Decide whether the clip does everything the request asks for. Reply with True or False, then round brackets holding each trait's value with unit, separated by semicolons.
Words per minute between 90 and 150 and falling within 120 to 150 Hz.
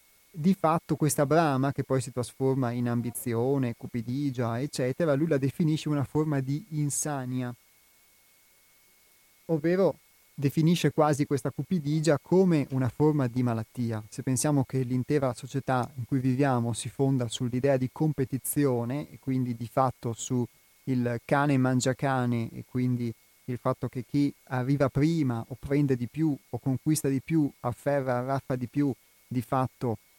True (145 wpm; 135 Hz)